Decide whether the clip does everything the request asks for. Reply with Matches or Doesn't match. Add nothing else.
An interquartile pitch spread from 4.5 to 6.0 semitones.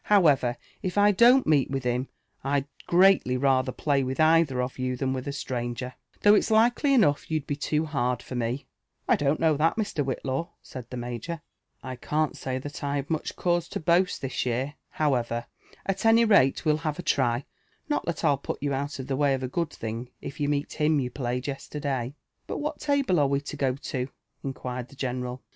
Doesn't match